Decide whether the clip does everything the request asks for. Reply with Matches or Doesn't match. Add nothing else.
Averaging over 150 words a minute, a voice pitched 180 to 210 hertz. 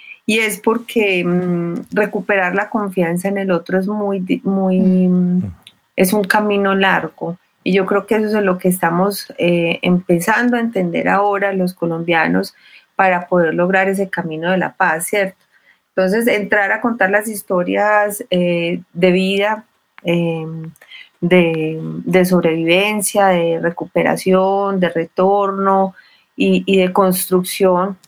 Doesn't match